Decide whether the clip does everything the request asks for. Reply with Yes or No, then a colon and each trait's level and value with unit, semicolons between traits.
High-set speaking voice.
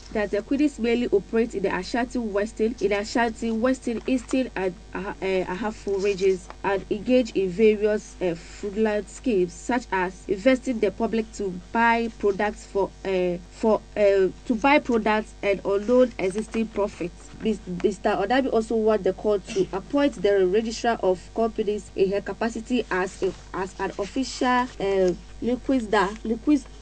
Yes: high, 210 Hz